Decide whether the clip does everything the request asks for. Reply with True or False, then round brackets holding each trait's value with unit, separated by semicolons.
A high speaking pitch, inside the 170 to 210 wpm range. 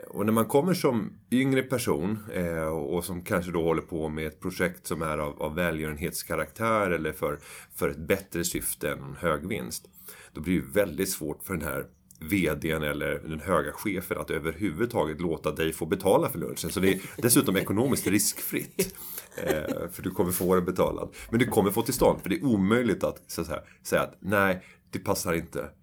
False (85 Hz; 190 wpm)